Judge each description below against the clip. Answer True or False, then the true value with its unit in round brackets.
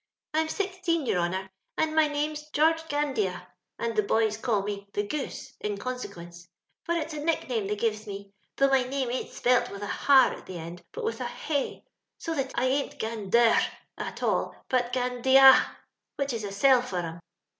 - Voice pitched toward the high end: True (250 Hz)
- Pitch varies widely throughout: True (6.1 semitones)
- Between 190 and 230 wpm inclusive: True (195 wpm)